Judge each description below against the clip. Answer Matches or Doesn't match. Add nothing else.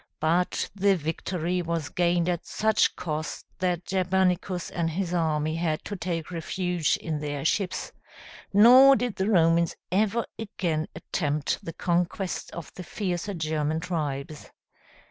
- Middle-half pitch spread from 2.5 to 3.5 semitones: Matches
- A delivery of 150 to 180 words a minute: Doesn't match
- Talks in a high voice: Doesn't match